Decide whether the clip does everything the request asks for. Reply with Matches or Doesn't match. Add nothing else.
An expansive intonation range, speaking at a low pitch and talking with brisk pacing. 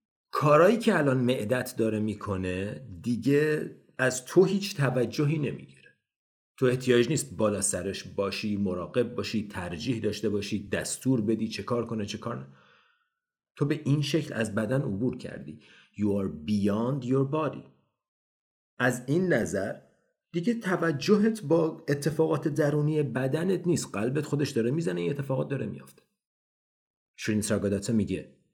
Doesn't match